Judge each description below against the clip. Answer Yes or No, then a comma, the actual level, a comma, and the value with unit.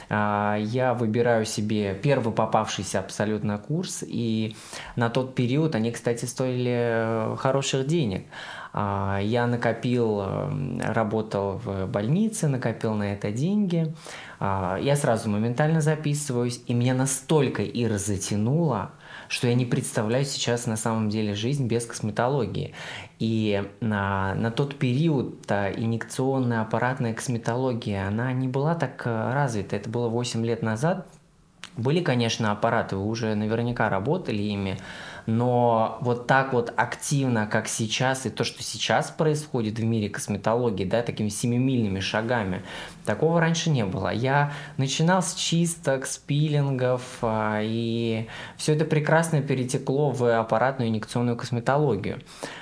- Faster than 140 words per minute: No, average, 125 wpm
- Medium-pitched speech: No, low, 120 Hz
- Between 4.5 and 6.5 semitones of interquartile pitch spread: No, average, 3.7 semitones